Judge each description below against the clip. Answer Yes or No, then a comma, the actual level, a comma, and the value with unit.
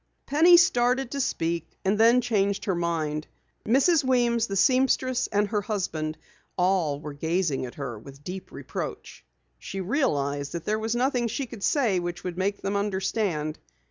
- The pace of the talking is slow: No, average, 165 wpm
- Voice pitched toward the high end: Yes, high, 195 Hz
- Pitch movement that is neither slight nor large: No, wide, 6.6 semitones